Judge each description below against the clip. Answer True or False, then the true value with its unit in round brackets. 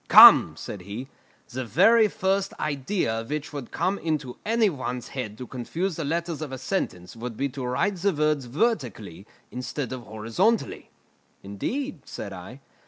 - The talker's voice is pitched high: False (140 Hz)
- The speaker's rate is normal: True (160 wpm)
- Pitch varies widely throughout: True (7.2 semitones)